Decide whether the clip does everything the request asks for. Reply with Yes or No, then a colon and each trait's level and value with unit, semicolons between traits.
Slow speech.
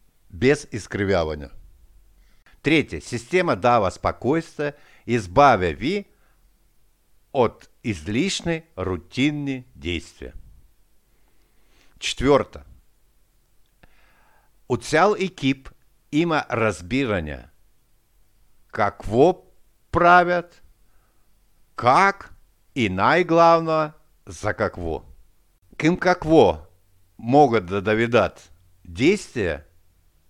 Yes: slow, 65 wpm